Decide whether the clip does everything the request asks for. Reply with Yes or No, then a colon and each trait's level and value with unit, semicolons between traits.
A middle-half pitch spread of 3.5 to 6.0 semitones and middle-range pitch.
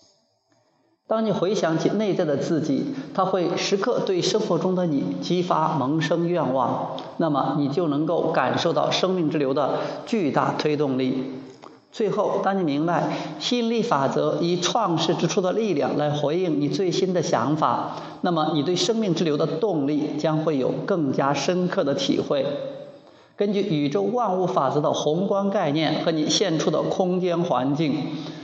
Yes: average, 4.1 semitones; medium, 170 Hz